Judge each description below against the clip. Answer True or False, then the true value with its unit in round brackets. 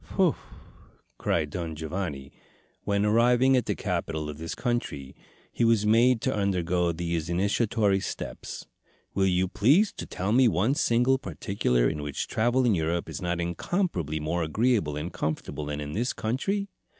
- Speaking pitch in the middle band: False (95 Hz)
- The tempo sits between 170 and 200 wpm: False (160 wpm)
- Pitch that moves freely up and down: True (6.7 semitones)